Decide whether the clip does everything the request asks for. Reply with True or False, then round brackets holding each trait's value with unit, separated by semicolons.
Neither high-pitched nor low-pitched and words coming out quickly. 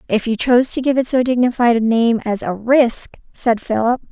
False (240 Hz; 220 wpm)